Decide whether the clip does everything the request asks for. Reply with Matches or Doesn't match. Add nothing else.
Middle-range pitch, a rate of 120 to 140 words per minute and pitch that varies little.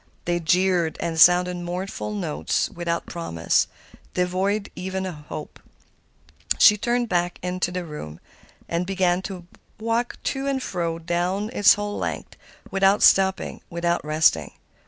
Matches